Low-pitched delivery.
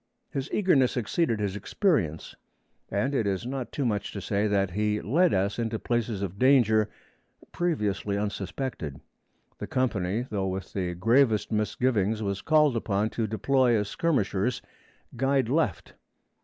Yes: low, 110 Hz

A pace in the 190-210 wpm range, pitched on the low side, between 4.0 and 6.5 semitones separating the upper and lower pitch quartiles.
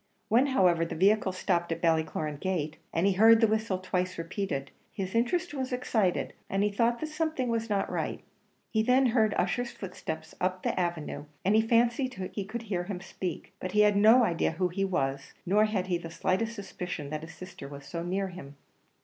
No: average, 200 wpm; high, 190 Hz; average, 4.5 semitones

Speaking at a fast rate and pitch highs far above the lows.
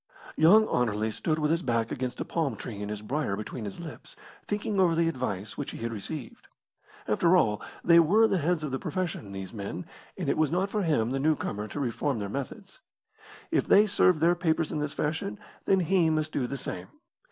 Yes: fast, 210 wpm; wide, 6.9 semitones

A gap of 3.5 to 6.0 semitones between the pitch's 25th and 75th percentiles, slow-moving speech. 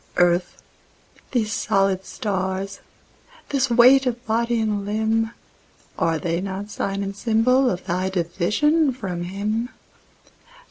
Yes: average, 3.8 semitones; slow, 110 wpm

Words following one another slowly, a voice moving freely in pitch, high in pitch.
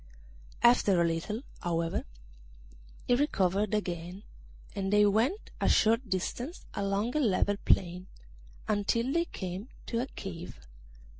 No: slow, 125 wpm; average, 4.6 semitones; high, 205 Hz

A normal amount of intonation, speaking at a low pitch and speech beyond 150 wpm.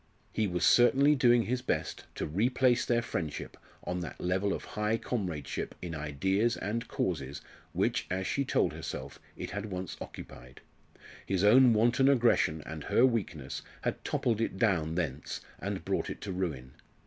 No: wide, 6.6 semitones; very low, 95 Hz; average, 160 wpm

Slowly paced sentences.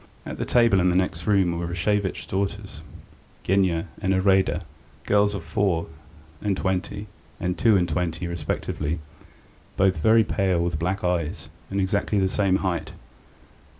No: average, 150 wpm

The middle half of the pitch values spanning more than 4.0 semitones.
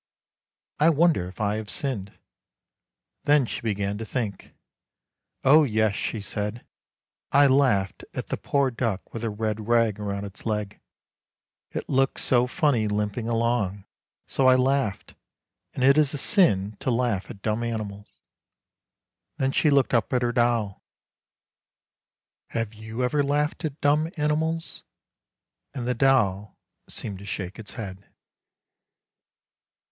Yes: average, 4.6 semitones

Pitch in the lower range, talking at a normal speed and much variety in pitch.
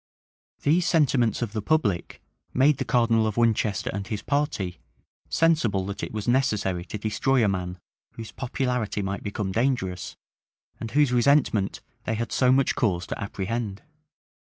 No: low, 115 Hz; average, 150 wpm; average, 4.7 semitones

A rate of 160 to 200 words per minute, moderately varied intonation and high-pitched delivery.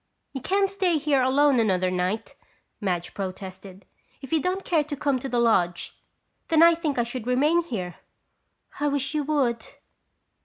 No: average, 165 wpm; wide, 7.2 semitones; very high, 265 Hz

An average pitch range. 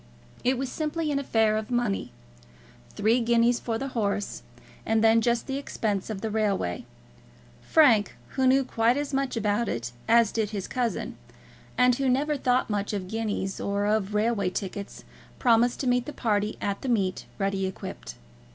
Yes: average, 3.5 semitones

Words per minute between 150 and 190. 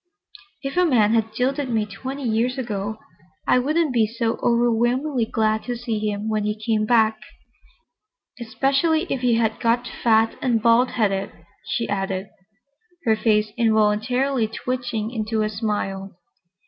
No: average, 140 wpm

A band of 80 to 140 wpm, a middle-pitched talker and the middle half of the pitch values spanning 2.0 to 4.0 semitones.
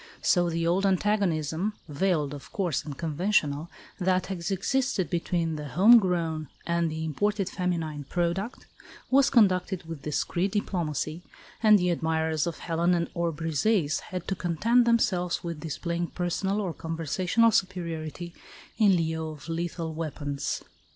Yes: slow, 135 wpm; medium, 170 Hz; average, 3.0 semitones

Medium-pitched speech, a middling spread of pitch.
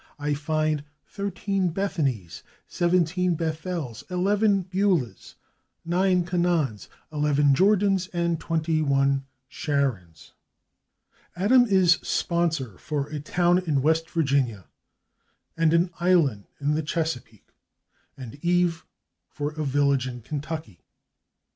Yes: medium, 160 Hz; average, 4.1 semitones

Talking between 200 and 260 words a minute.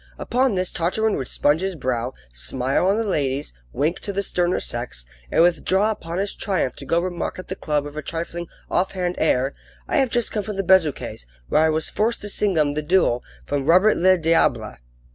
Yes: fast, 205 wpm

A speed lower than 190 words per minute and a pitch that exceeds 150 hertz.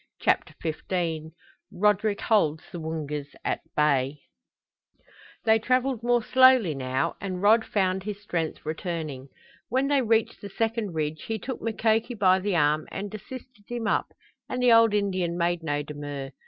Yes: average, 155 wpm; high, 190 Hz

